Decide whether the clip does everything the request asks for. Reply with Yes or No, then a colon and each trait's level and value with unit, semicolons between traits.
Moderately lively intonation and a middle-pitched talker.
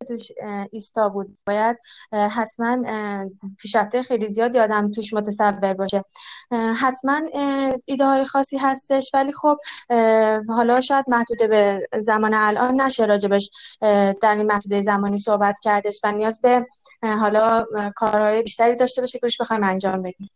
No: average, 3.2 semitones; high, 220 Hz